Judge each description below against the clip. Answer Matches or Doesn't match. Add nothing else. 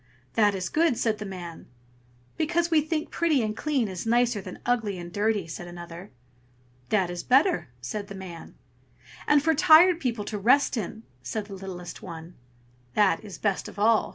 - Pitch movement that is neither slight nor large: Doesn't match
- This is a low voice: Doesn't match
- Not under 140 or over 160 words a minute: Doesn't match